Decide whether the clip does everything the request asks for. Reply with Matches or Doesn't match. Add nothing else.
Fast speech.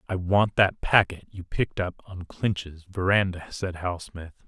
Doesn't match